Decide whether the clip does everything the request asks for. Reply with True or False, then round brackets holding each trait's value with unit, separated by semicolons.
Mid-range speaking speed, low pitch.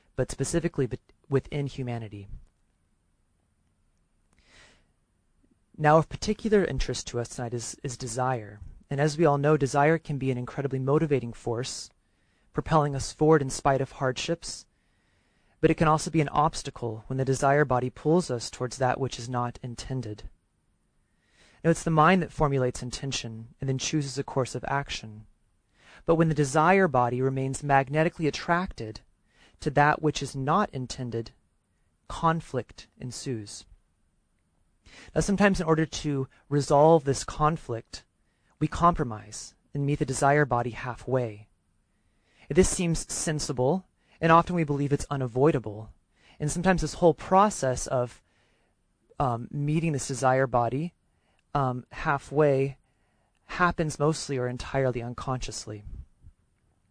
False (130 wpm; 130 Hz)